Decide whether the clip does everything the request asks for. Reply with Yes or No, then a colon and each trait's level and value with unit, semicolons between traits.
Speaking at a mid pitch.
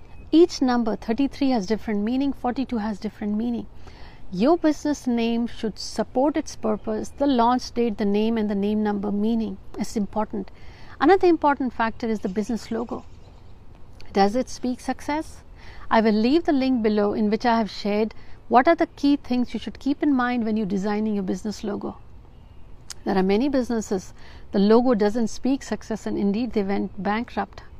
No: high, 225 Hz